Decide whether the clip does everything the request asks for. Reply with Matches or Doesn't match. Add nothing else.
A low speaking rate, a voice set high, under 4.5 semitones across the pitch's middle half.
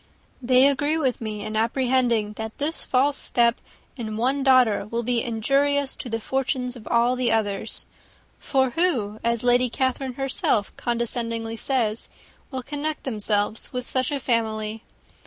Doesn't match